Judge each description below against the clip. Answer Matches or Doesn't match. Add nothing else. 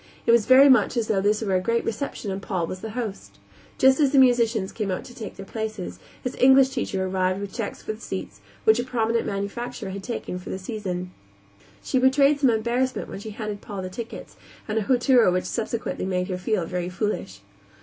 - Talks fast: Matches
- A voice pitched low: Doesn't match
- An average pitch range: Matches